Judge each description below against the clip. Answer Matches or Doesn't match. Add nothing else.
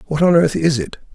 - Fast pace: Matches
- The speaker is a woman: Doesn't match